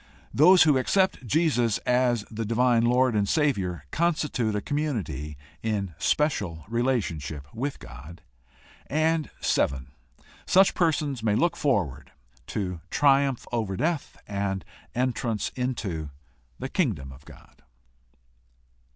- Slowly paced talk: Yes, slow, 110 wpm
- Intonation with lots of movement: Yes, wide, 7.0 semitones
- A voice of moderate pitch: No, low, 115 Hz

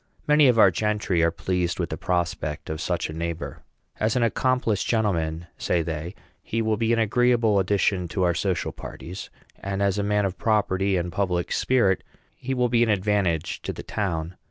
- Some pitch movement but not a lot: Yes, average, 4.1 semitones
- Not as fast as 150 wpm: No, average, 190 wpm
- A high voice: No, very low, 95 Hz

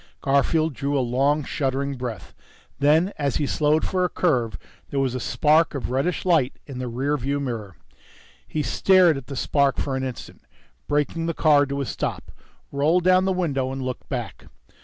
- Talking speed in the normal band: Yes, average, 185 wpm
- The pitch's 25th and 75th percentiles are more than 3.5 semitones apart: No, average, 3.0 semitones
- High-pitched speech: No, medium, 140 Hz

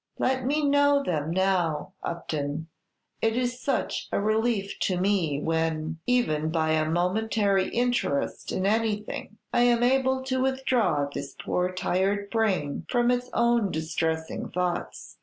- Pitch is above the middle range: Yes, high, 200 Hz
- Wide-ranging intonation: Yes, wide, 7.0 semitones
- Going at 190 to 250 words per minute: No, average, 140 wpm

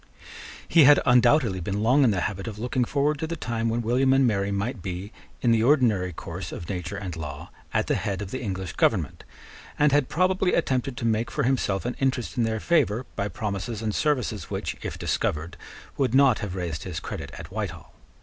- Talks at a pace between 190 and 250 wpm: Yes, fast, 205 wpm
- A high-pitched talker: No, low, 115 Hz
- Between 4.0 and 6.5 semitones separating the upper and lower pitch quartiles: Yes, average, 5.2 semitones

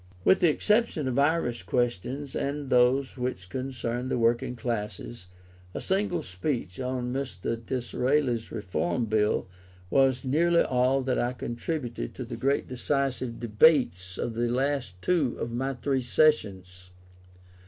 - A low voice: Yes, low, 125 Hz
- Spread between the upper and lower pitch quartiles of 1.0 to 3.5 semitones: Yes, average, 3.0 semitones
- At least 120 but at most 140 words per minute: Yes, slow, 135 wpm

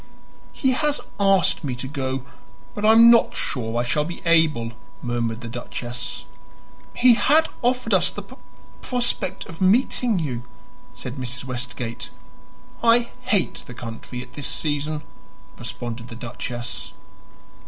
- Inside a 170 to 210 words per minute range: No, average, 140 wpm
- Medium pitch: Yes, medium, 145 Hz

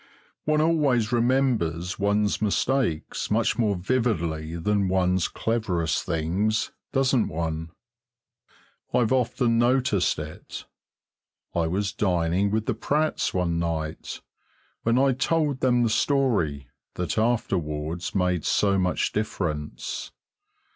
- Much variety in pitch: Yes, wide, 6.4 semitones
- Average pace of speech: No, slow, 110 wpm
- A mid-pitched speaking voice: No, low, 100 Hz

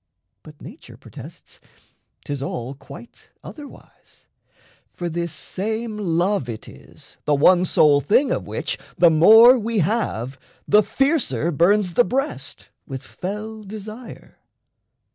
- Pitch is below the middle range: No, medium, 185 Hz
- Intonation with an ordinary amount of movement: No, wide, 6.8 semitones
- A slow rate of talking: Yes, slow, 125 wpm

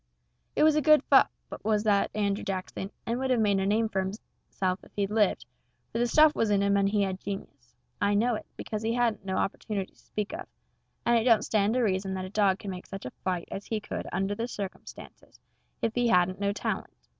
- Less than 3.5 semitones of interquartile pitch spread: Yes, average, 2.9 semitones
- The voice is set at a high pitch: Yes, high, 205 Hz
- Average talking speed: No, fast, 230 wpm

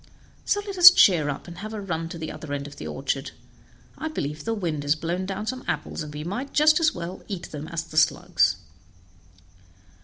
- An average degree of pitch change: No, wide, 6.4 semitones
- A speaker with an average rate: No, fast, 215 wpm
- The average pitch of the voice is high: No, medium, 170 Hz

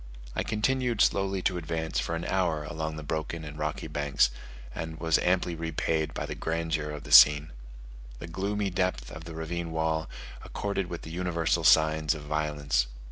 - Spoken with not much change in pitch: Yes, narrow, 2.3 semitones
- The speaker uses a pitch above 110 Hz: No, very low, 80 Hz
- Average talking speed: Yes, average, 175 wpm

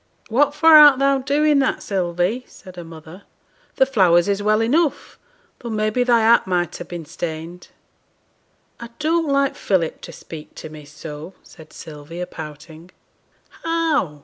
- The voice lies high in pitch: Yes, high, 195 Hz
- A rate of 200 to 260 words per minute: No, average, 155 wpm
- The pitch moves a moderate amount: No, wide, 8.6 semitones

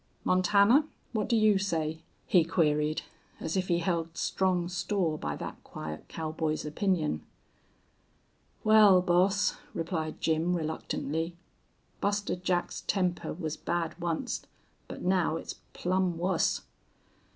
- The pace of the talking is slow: Yes, slow, 120 wpm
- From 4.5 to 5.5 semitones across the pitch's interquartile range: No, average, 2.9 semitones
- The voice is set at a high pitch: No, medium, 175 Hz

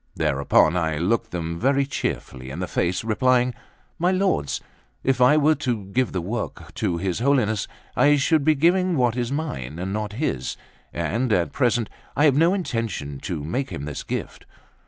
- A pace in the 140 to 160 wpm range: No, average, 175 wpm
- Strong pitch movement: Yes, wide, 8.1 semitones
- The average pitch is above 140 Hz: No, low, 115 Hz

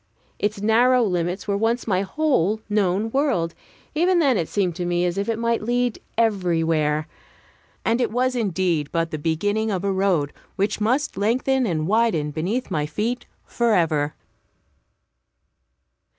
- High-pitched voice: Yes, high, 205 Hz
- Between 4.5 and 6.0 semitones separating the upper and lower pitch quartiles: Yes, wide, 5.4 semitones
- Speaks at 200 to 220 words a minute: No, average, 150 wpm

